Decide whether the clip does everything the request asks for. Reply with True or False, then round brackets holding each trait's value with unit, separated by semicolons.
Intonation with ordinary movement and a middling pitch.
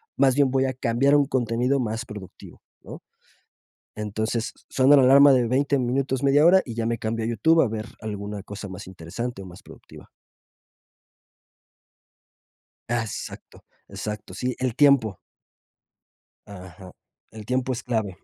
False (4.0 semitones; 120 Hz)